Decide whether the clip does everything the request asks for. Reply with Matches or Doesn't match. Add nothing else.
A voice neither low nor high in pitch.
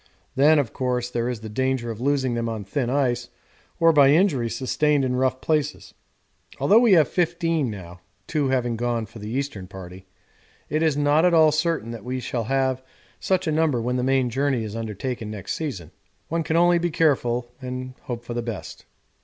Doesn't match